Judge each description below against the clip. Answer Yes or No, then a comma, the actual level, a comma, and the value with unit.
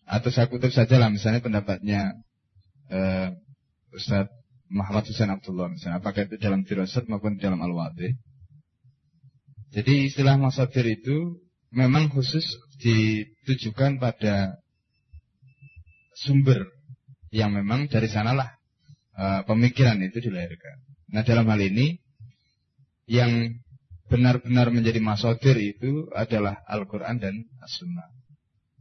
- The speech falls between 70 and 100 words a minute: No, average, 110 wpm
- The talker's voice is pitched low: Yes, low, 115 Hz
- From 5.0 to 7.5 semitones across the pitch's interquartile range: No, average, 4.2 semitones